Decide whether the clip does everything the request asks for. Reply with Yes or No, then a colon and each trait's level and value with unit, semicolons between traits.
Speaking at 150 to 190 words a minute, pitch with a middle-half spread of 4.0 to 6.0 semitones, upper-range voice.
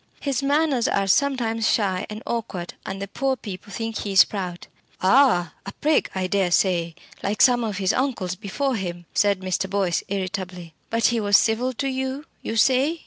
Yes: average, 180 wpm; average, 5.2 semitones; high, 205 Hz